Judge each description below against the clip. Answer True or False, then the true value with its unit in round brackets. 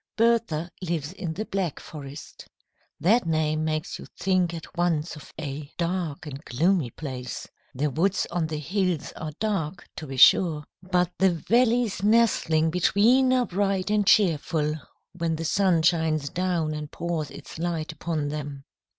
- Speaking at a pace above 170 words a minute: False (155 wpm)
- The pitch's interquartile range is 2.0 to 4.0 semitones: True (3.6 semitones)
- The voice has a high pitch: False (165 Hz)